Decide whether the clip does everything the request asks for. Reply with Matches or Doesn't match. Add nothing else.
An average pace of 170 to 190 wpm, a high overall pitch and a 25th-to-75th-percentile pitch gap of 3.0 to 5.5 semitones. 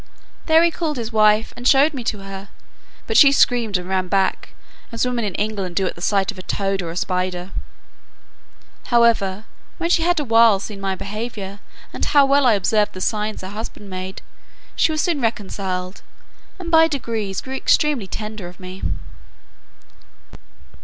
Matches